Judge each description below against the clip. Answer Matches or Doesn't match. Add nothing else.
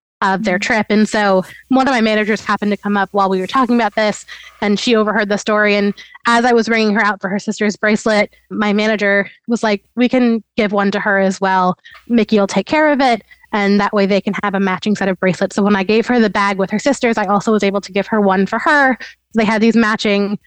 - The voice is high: Matches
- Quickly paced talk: Matches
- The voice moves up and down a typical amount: Doesn't match